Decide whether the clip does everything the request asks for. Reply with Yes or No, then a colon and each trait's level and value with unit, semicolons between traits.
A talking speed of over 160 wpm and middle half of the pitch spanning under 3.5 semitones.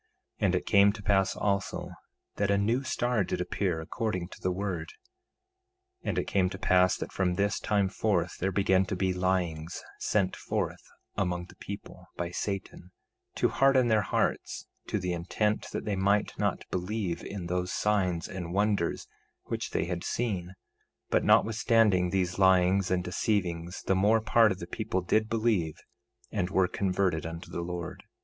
Yes: average, 170 wpm; narrow, 2.5 semitones